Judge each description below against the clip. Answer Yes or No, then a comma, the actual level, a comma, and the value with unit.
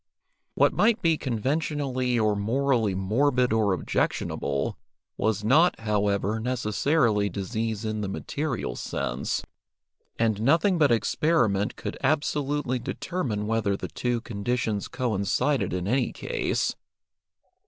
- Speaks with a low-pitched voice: Yes, low, 115 Hz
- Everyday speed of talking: No, slow, 110 wpm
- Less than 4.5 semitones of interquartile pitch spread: No, average, 5.0 semitones